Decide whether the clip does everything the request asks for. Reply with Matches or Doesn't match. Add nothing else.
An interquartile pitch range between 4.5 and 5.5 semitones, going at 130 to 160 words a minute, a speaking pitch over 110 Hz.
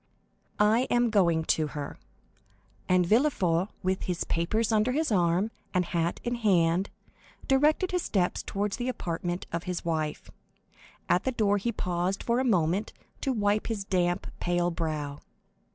Matches